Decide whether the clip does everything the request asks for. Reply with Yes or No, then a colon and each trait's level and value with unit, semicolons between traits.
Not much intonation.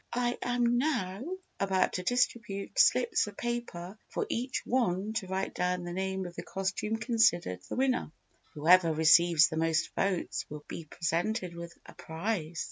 No: average, 5.2 semitones